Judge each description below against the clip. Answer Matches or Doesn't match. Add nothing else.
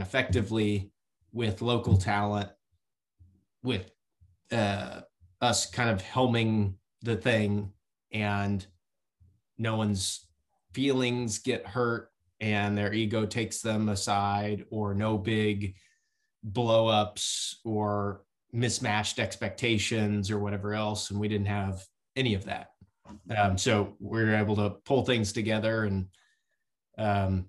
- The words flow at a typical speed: Doesn't match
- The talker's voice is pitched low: Matches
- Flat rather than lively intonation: Matches